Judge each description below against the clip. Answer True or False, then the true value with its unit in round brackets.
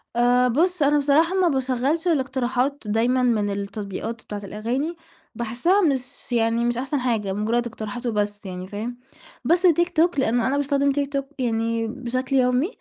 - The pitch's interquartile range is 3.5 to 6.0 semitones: True (3.9 semitones)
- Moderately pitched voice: False (250 Hz)